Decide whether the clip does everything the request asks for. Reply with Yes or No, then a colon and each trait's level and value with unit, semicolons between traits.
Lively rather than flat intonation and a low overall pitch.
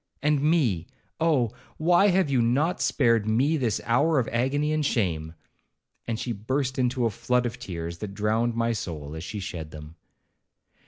Yes: wide, 5.8 semitones; low, 120 Hz